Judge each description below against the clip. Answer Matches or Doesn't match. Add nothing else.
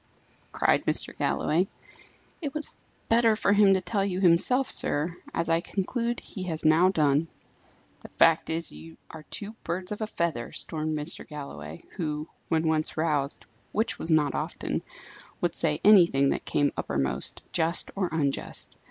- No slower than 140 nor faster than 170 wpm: Matches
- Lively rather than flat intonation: Doesn't match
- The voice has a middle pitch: Matches